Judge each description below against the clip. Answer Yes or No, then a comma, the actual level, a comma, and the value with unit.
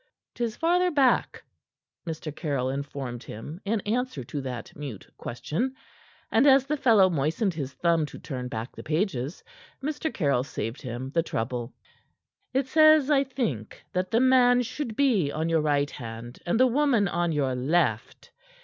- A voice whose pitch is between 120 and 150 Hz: No, medium, 165 Hz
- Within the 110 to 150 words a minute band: No, average, 160 wpm